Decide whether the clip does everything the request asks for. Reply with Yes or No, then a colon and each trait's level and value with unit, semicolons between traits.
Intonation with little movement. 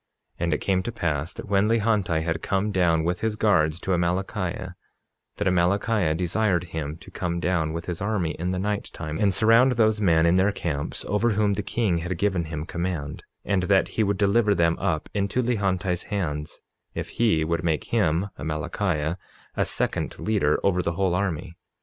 No: average, 3.7 semitones